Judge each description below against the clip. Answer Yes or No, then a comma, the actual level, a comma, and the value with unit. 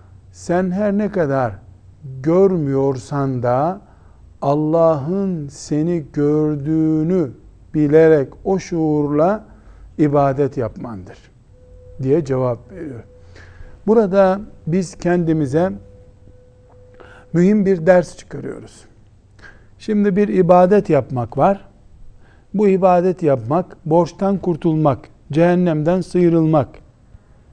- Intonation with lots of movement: Yes, wide, 6.8 semitones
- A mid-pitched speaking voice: Yes, medium, 150 Hz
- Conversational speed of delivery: No, slow, 80 wpm